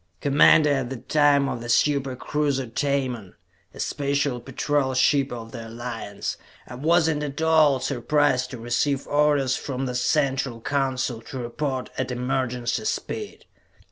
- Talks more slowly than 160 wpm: Yes, average, 145 wpm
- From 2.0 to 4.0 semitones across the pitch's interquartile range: Yes, average, 2.8 semitones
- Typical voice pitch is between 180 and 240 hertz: No, low, 135 Hz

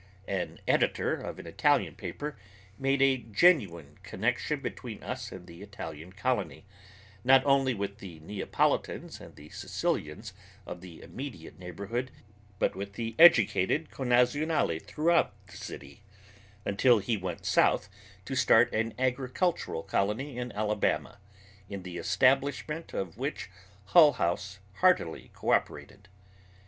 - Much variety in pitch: Yes, wide, 6.2 semitones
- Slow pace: Yes, slow, 125 wpm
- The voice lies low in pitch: Yes, low, 110 Hz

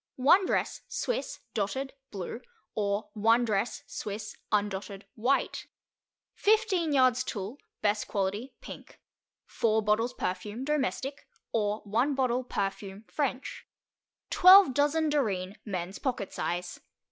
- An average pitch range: Yes, average, 5.0 semitones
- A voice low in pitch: No, high, 225 Hz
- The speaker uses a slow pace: Yes, slow, 110 wpm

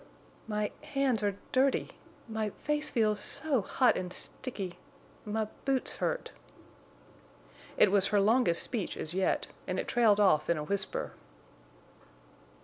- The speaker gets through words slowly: Yes, slow, 125 wpm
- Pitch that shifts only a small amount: No, average, 4.7 semitones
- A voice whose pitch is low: No, high, 215 Hz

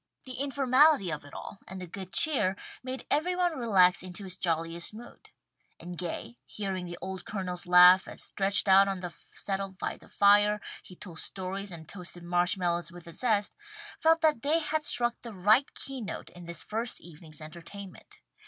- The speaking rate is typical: Yes, average, 185 wpm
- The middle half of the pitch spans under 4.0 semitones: No, average, 4.8 semitones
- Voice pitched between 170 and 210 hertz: Yes, high, 190 Hz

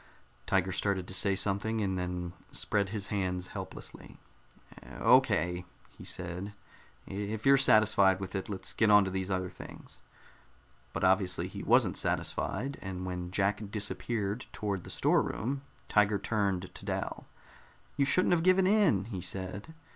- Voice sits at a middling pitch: No, low, 100 Hz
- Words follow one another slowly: No, average, 145 wpm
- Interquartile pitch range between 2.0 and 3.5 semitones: Yes, narrow, 2.6 semitones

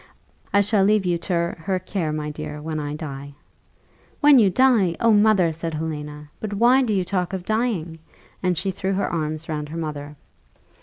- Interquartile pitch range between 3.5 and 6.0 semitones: Yes, average, 4.8 semitones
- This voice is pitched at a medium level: Yes, medium, 175 Hz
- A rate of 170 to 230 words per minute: Yes, average, 190 wpm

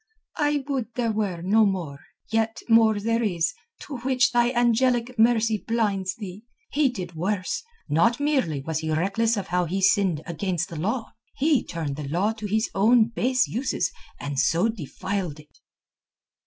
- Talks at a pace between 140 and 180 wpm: Yes, average, 165 wpm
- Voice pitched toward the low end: No, high, 215 Hz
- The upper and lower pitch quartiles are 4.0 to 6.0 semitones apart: Yes, average, 5.1 semitones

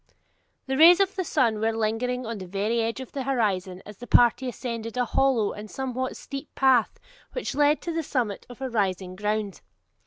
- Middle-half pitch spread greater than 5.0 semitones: No, average, 3.9 semitones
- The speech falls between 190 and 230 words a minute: Yes, average, 195 wpm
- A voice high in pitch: Yes, high, 240 Hz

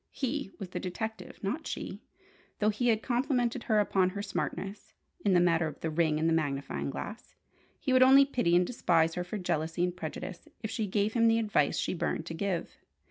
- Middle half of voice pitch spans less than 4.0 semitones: No, average, 5.2 semitones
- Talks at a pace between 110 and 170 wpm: No, fast, 205 wpm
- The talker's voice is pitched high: Yes, high, 195 Hz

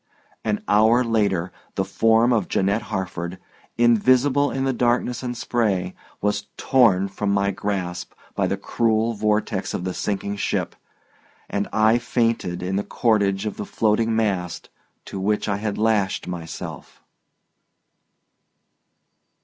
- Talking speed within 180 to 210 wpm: No, slow, 135 wpm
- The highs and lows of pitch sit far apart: No, average, 2.9 semitones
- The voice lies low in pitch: Yes, low, 105 Hz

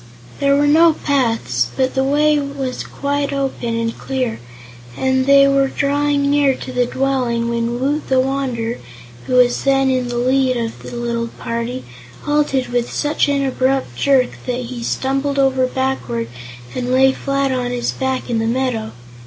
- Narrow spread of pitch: Yes, narrow, 2.3 semitones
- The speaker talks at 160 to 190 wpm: Yes, average, 170 wpm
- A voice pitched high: Yes, very high, 260 Hz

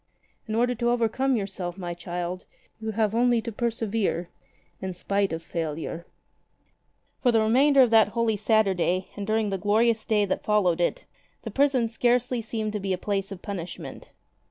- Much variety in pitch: No, average, 3.6 semitones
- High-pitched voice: Yes, high, 215 Hz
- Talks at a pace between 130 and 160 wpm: No, average, 170 wpm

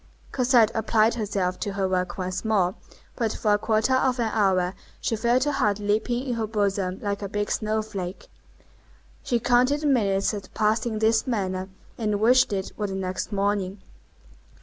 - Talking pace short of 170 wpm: No, average, 180 wpm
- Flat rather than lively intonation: No, average, 3.0 semitones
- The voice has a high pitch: Yes, high, 210 Hz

